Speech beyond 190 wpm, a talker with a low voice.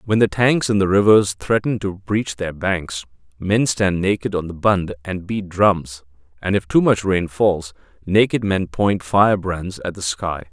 No: average, 185 wpm; very low, 95 Hz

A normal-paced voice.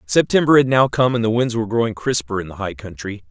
No: fast, 255 wpm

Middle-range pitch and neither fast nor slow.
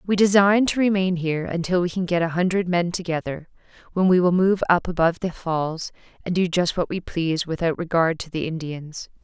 No: medium, 175 Hz; fast, 210 wpm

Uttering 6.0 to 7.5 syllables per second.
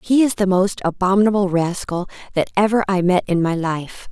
No: 5.4 syllables/s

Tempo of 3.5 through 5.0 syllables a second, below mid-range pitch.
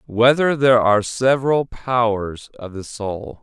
Yes: 4.4 syllables/s; low, 115 Hz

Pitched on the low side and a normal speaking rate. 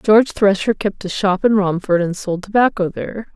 No: high, 200 Hz; average, 195 wpm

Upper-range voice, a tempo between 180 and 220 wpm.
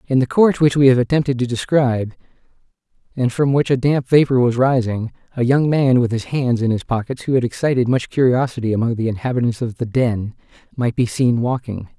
No: low, 125 Hz; fast, 205 wpm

